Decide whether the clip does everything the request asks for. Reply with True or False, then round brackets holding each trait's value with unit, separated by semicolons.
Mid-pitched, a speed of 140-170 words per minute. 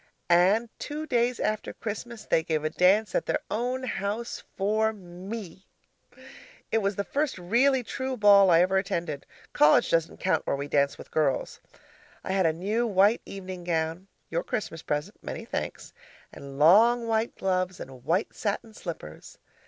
False (195 Hz; 160 wpm)